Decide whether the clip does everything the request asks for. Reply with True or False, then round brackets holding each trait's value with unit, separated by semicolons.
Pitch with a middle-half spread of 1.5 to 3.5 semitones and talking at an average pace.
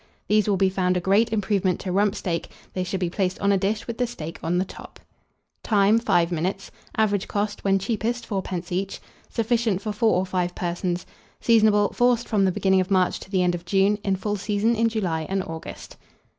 False (2.8 semitones; 210 wpm)